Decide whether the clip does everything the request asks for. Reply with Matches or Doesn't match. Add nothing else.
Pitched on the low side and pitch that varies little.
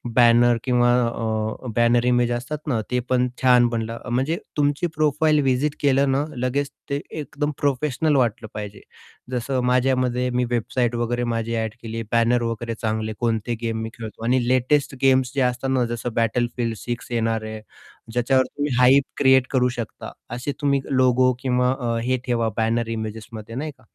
Matches